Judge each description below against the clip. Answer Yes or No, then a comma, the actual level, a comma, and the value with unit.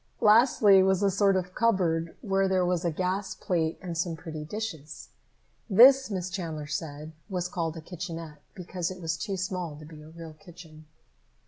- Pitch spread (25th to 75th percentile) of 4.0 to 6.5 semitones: No, average, 3.0 semitones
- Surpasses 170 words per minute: Yes, average, 180 wpm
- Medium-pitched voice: Yes, medium, 180 Hz